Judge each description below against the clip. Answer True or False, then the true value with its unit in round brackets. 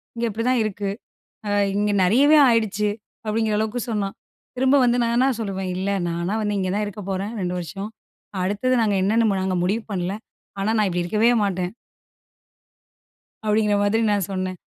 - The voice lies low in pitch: False (205 Hz)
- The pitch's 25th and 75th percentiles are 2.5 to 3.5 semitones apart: True (2.8 semitones)